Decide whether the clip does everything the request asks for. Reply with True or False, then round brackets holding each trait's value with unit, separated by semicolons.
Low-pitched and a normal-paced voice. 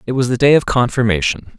False (125 Hz; 225 wpm)